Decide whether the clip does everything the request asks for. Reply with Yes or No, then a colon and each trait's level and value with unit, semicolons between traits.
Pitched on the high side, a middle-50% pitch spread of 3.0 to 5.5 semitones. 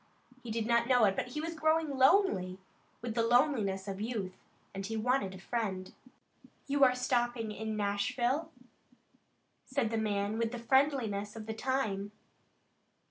Yes: high, 230 Hz; average, 4.1 semitones